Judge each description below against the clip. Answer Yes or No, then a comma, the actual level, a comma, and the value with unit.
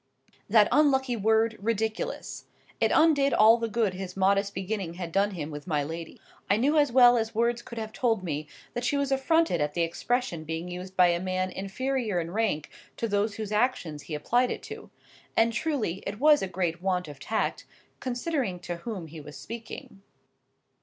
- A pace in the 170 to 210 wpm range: Yes, average, 185 wpm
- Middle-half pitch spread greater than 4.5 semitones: Yes, average, 5.2 semitones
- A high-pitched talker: Yes, high, 210 Hz